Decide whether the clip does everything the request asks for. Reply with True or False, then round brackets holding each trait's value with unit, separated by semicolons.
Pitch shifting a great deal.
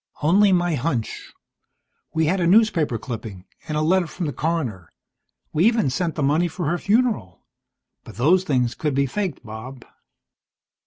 True (5.9 semitones)